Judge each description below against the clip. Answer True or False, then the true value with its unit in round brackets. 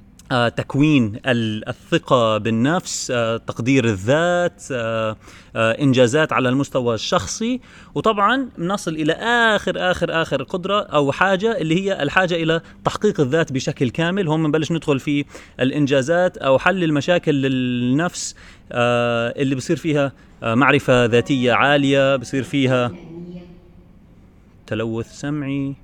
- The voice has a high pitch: False (140 Hz)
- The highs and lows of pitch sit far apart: True (5.7 semitones)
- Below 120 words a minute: True (105 wpm)